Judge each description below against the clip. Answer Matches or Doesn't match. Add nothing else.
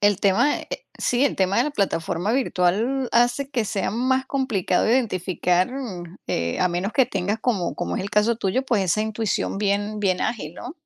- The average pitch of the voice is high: Matches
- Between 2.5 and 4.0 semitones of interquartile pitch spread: Doesn't match